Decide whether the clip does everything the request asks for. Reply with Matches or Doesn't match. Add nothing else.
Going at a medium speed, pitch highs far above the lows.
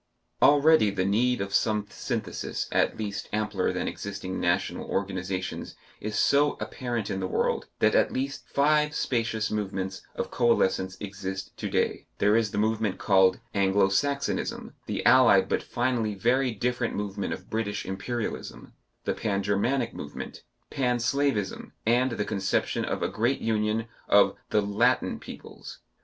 Doesn't match